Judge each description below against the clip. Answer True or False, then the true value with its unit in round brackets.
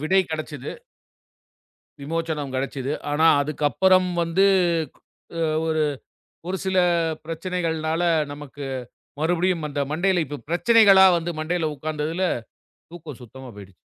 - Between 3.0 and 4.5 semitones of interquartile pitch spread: True (3.3 semitones)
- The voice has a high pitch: False (160 Hz)